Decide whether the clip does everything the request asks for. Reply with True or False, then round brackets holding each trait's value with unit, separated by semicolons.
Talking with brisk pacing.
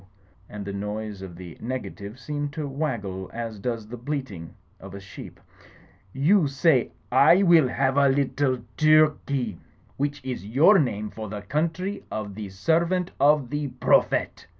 False (155 wpm)